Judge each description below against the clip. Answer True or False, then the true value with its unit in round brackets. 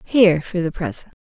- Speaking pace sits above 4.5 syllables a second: True (5.7 syllables/s)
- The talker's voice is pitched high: False (175 Hz)